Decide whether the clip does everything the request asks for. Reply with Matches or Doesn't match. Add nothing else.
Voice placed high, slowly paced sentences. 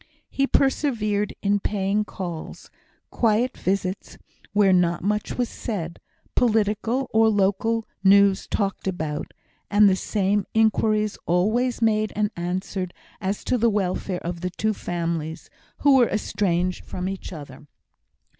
Matches